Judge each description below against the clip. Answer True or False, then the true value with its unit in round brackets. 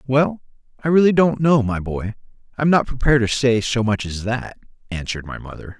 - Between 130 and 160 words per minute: False (205 wpm)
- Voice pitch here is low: True (125 Hz)